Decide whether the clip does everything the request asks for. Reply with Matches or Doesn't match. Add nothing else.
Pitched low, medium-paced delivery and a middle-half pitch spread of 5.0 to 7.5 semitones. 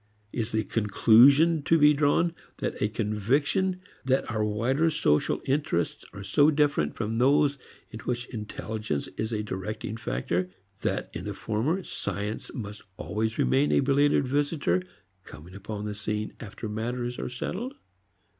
Matches